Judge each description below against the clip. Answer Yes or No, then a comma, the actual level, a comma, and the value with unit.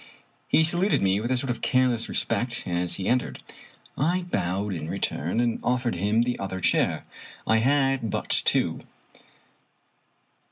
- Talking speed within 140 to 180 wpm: Yes, average, 155 wpm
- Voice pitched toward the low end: Yes, low, 120 Hz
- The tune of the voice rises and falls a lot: No, average, 5.0 semitones